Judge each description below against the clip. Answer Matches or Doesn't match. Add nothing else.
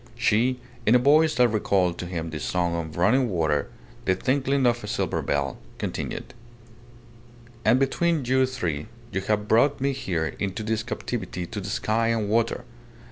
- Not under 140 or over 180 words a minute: Matches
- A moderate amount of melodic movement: Doesn't match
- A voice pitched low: Matches